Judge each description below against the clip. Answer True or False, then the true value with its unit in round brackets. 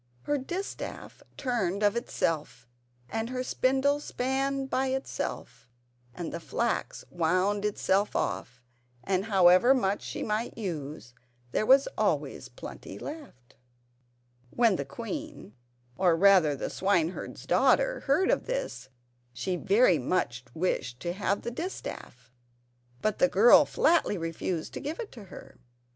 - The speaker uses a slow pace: True (125 wpm)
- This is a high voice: True (200 Hz)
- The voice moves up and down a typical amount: False (7.9 semitones)